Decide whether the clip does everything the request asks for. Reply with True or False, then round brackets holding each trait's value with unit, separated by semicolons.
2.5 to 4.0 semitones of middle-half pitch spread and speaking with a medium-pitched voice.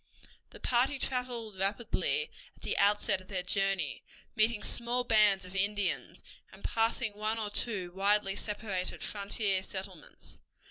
False (2.8 semitones; 205 Hz)